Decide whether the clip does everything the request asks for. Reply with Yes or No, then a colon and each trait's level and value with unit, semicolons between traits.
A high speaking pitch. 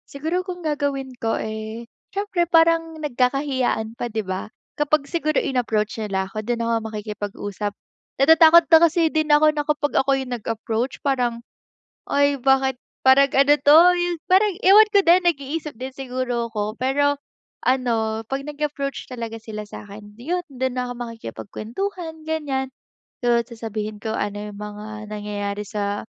Yes: very high, 255 Hz